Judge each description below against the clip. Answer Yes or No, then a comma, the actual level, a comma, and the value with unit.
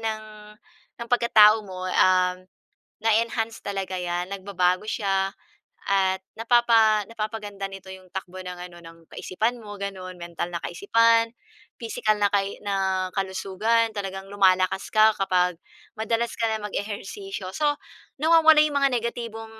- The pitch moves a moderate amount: Yes, average, 3.2 semitones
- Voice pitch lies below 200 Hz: No, high, 205 Hz